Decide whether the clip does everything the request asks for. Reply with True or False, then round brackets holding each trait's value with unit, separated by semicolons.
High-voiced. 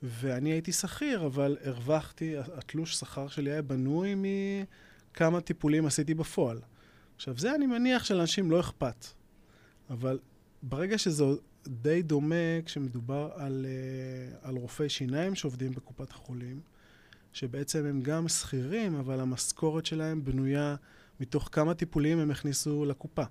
False (145 Hz)